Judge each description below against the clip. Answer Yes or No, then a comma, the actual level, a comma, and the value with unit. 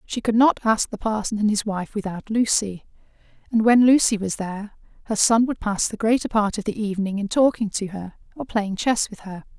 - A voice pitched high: Yes, high, 215 Hz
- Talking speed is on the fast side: Yes, fast, 220 wpm